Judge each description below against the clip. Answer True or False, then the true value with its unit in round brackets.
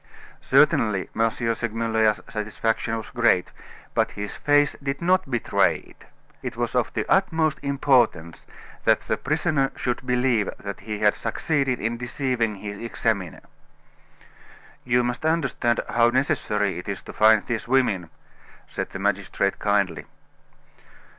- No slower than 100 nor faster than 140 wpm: True (135 wpm)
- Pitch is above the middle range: False (115 Hz)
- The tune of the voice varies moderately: True (4.2 semitones)